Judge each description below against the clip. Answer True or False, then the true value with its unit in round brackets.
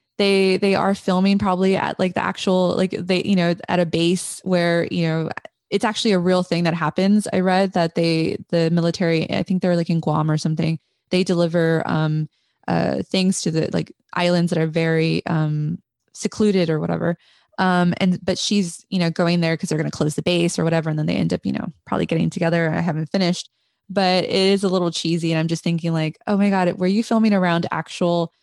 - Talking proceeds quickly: True (220 wpm)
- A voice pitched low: False (175 Hz)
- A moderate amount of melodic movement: False (2.3 semitones)